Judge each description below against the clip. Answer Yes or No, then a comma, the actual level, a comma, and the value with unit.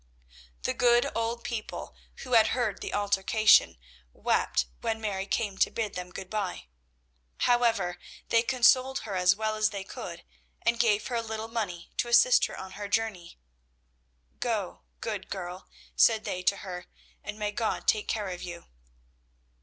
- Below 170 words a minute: Yes, average, 160 wpm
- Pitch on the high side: Yes, high, 215 Hz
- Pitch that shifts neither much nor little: Yes, average, 3.1 semitones